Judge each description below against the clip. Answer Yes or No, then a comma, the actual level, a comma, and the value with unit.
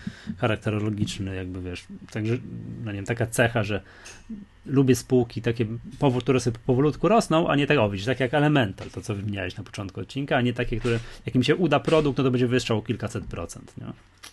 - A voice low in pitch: Yes, low, 120 Hz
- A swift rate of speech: Yes, fast, 185 wpm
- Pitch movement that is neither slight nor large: Yes, average, 4.0 semitones